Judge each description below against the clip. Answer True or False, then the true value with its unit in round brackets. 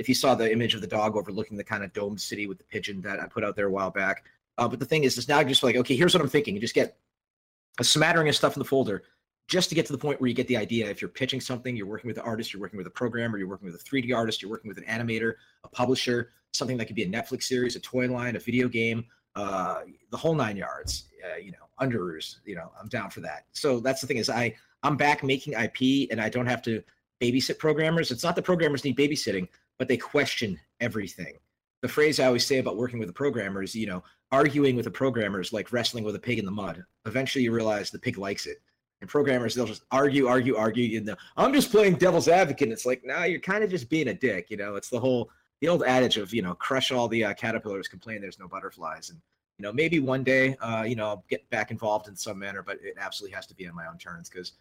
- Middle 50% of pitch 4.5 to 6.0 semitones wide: False (3.9 semitones)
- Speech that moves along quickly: True (270 wpm)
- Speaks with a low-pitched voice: True (125 Hz)